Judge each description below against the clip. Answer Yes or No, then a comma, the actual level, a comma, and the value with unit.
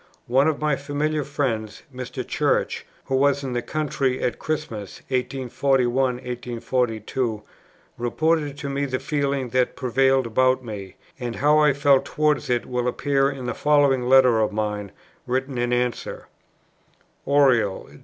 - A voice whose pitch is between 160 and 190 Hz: No, low, 130 Hz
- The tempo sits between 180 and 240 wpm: No, average, 145 wpm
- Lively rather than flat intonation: No, narrow, 2.5 semitones